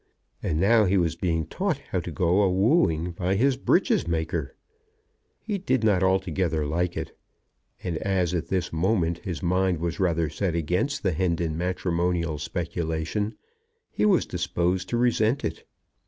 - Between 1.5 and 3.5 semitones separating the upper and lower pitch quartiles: Yes, average, 2.7 semitones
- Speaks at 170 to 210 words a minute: No, average, 155 wpm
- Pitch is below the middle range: Yes, very low, 90 Hz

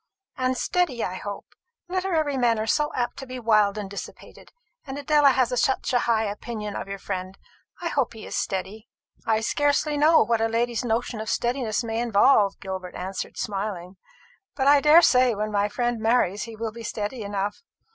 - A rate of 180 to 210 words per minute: Yes, average, 185 wpm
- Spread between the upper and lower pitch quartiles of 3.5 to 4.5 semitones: Yes, average, 4.1 semitones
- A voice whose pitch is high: Yes, high, 230 Hz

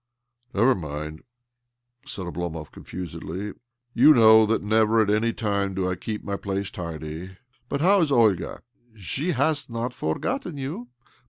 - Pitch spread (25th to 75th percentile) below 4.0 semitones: No, average, 5.0 semitones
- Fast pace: No, average, 160 wpm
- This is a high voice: No, low, 110 Hz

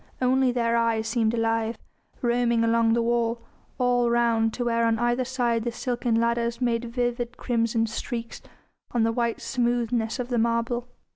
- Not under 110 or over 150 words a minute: No, average, 160 wpm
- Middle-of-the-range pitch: No, high, 235 Hz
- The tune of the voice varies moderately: No, narrow, 0.9 semitones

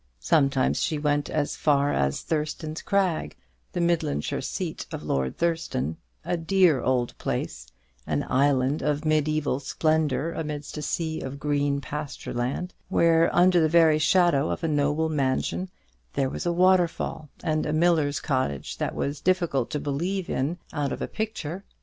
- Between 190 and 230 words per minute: No, average, 155 wpm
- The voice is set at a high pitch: No, medium, 150 Hz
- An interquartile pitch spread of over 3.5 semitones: No, average, 3.2 semitones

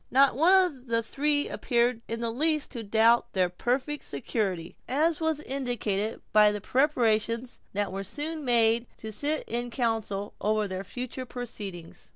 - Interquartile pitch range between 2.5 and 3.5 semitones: No, average, 4.4 semitones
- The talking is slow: No, average, 160 wpm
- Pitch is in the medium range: No, high, 235 Hz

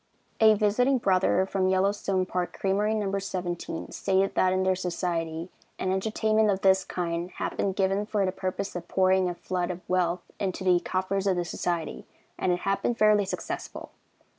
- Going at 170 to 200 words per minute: Yes, average, 180 wpm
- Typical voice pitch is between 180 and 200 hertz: Yes, high, 190 Hz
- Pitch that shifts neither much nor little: No, narrow, 1.7 semitones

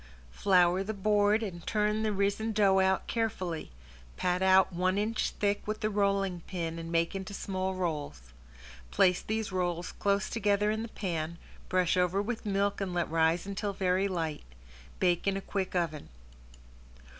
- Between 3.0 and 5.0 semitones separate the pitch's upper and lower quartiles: No, narrow, 2.5 semitones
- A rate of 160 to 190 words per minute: Yes, average, 165 wpm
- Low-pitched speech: No, high, 190 Hz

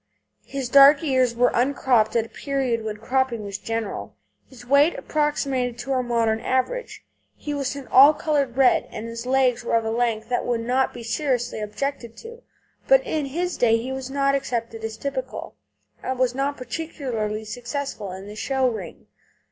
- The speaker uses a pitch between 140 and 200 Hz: No, very high, 250 Hz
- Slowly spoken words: No, average, 185 wpm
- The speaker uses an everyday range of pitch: Yes, average, 3.2 semitones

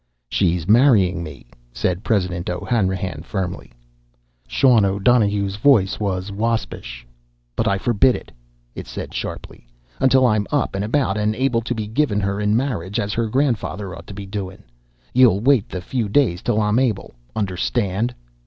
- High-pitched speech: No, low, 105 Hz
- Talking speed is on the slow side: No, average, 155 wpm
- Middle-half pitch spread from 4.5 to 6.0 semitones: No, average, 3.9 semitones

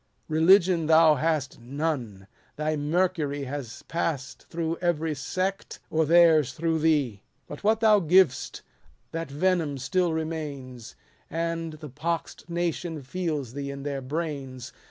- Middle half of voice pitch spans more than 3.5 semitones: No, average, 3.2 semitones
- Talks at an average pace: No, slow, 130 wpm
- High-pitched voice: No, medium, 155 Hz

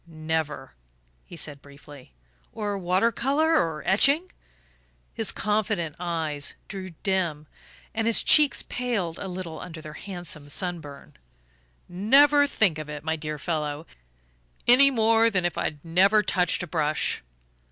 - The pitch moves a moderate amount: No, wide, 5.8 semitones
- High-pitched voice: No, medium, 175 Hz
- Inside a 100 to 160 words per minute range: Yes, slow, 135 wpm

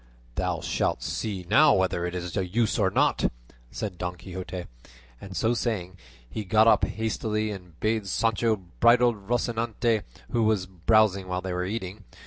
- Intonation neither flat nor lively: Yes, average, 3.4 semitones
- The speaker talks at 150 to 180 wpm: Yes, average, 160 wpm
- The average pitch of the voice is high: No, low, 100 Hz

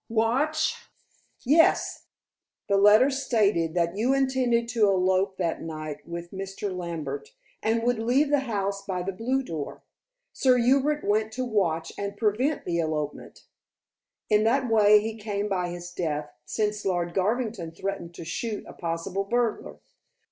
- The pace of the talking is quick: No, average, 150 wpm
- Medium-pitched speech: No, high, 205 Hz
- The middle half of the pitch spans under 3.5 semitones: No, wide, 5.4 semitones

